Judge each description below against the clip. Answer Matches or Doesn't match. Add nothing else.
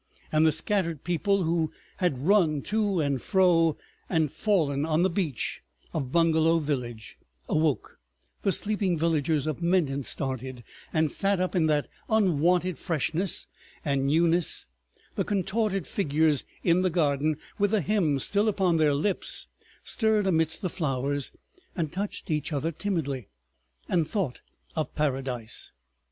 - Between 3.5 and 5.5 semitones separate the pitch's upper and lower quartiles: Matches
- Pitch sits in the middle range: Matches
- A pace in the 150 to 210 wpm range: Doesn't match